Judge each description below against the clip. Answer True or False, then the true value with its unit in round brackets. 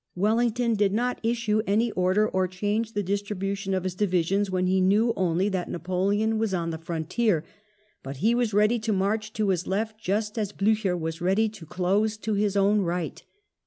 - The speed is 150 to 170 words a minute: False (190 wpm)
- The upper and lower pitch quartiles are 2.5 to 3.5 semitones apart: True (2.8 semitones)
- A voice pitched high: True (200 Hz)